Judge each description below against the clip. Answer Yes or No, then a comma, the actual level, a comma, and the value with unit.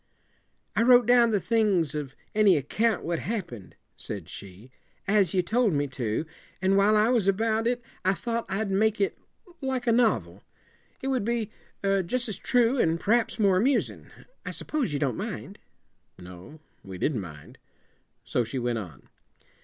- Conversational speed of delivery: Yes, average, 165 wpm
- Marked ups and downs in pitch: Yes, wide, 9.0 semitones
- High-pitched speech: Yes, high, 195 Hz